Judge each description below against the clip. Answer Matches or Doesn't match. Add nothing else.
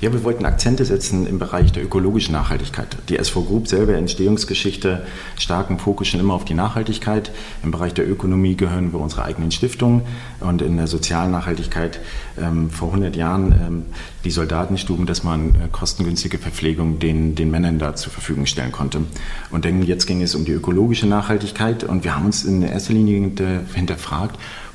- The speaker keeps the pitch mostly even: Doesn't match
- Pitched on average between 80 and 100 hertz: Matches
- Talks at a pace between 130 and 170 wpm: Doesn't match